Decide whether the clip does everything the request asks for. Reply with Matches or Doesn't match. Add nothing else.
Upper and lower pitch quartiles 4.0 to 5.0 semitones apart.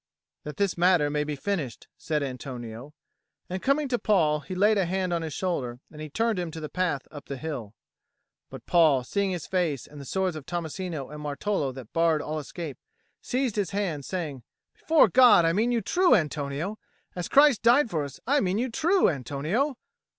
Doesn't match